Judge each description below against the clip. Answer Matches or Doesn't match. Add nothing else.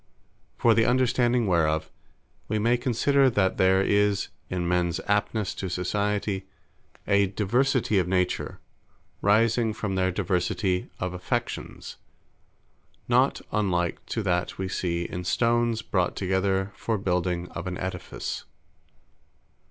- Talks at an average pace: Doesn't match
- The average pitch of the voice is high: Doesn't match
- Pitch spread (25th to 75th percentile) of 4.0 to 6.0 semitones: Doesn't match